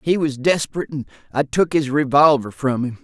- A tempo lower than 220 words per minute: Yes, average, 200 wpm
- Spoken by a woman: No, male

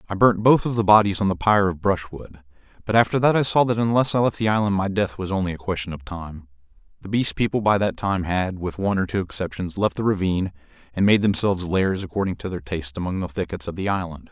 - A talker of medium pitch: No, very low, 95 Hz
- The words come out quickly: Yes, fast, 245 wpm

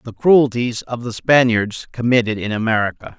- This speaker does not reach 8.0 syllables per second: Yes, 5.0 syllables/s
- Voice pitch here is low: Yes, low, 120 Hz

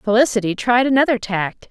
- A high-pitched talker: Yes, high, 230 Hz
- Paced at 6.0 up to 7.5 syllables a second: No, 5.6 syllables/s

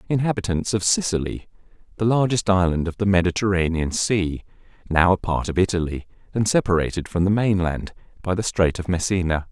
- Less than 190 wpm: Yes, average, 160 wpm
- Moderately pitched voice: No, very low, 95 Hz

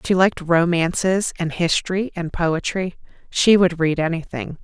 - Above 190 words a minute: No, average, 140 wpm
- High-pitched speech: No, medium, 175 Hz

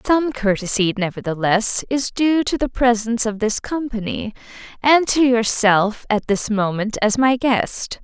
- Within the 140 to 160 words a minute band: Yes, average, 150 wpm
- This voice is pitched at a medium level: No, high, 230 Hz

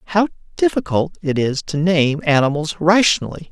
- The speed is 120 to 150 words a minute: Yes, slow, 135 wpm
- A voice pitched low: No, medium, 155 Hz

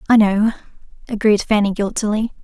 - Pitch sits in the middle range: No, high, 210 Hz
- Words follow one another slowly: Yes, slow, 125 wpm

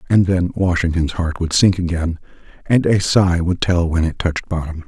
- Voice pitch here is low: Yes, very low, 85 Hz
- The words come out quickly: No, average, 195 wpm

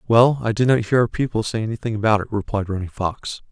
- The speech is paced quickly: Yes, fast, 240 wpm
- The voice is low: Yes, low, 110 Hz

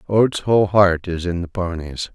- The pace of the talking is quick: No, average, 195 wpm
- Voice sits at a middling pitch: No, very low, 90 Hz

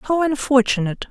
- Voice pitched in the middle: No, very high, 260 Hz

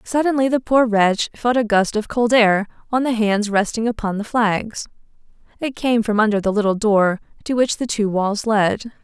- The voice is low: No, high, 220 Hz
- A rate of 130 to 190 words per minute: No, average, 200 wpm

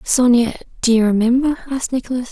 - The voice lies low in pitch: No, high, 245 Hz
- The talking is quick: No, average, 155 wpm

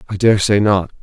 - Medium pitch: No, low, 100 Hz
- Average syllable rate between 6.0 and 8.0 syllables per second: No, 5.3 syllables/s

